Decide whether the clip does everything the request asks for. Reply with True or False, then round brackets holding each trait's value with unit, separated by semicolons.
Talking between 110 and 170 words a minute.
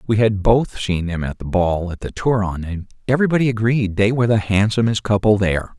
False (205 wpm)